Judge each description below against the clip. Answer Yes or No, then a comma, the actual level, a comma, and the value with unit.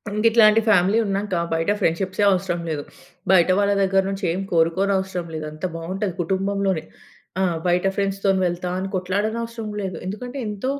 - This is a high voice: Yes, high, 195 Hz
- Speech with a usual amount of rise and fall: No, narrow, 2.3 semitones